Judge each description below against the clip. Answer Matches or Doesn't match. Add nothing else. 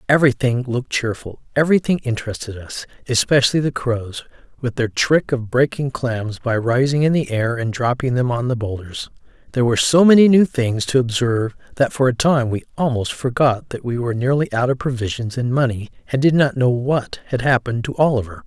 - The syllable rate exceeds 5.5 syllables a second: Matches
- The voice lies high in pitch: Doesn't match